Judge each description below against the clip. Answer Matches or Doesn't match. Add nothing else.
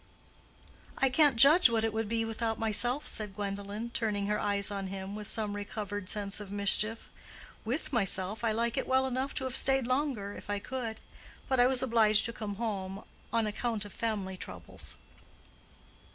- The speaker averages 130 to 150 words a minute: Doesn't match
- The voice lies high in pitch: Matches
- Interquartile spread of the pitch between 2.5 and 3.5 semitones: Matches